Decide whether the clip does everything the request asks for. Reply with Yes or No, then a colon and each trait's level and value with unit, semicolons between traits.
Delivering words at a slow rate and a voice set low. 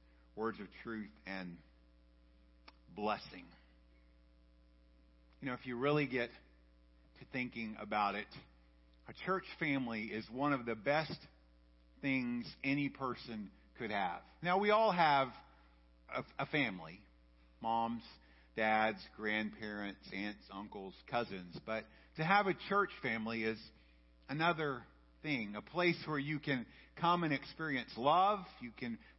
Yes: slow, 125 wpm; low, 110 Hz